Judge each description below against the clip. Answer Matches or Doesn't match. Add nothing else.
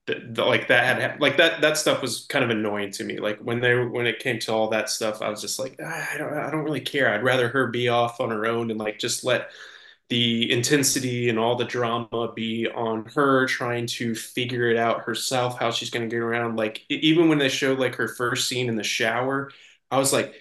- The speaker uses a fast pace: Matches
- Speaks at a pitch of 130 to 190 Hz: Doesn't match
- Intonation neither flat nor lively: Doesn't match